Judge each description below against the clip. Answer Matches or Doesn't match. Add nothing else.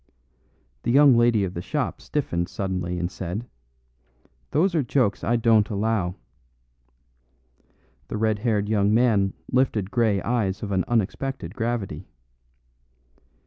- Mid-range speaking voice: Doesn't match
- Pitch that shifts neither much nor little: Matches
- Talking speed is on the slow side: Matches